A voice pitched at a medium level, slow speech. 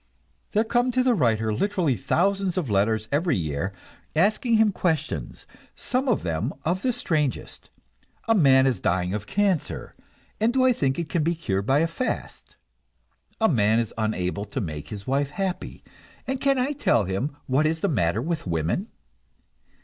No: medium, 150 Hz; average, 170 wpm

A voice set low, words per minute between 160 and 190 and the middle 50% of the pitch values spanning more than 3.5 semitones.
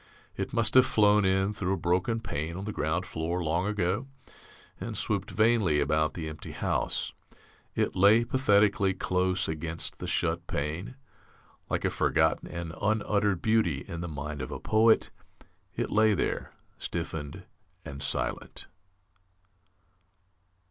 No: very low, 90 Hz; average, 140 wpm; average, 4.7 semitones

